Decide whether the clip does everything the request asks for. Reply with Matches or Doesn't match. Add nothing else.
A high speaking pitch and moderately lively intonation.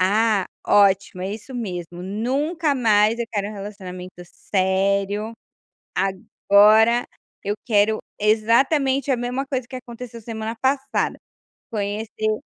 Matches